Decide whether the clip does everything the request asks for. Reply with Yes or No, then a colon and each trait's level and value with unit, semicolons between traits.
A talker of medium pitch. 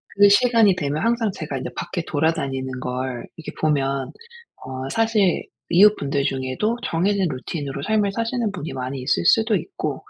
Yes: medium, 165 Hz